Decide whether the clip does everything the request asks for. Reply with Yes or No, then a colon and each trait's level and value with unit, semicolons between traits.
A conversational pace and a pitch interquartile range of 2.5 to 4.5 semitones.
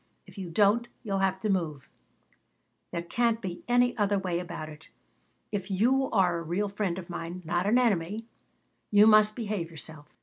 Yes: average, 175 wpm; average, 3.8 semitones